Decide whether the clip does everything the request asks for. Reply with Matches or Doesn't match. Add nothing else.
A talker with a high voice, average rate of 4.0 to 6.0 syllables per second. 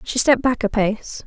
Matches